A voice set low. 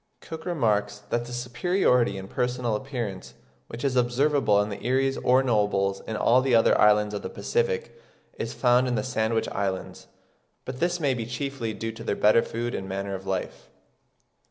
Yes: low, 120 Hz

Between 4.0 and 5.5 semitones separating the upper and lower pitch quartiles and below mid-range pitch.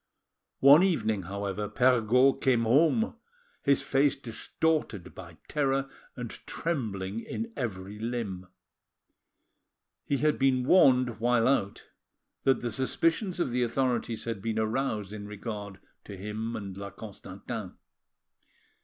Yes: average, 4.6 semitones; low, 115 Hz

